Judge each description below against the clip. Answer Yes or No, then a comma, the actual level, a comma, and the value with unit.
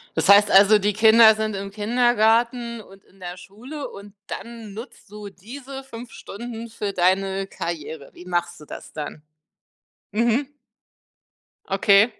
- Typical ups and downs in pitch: Yes, average, 3.2 semitones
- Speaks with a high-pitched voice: Yes, high, 210 Hz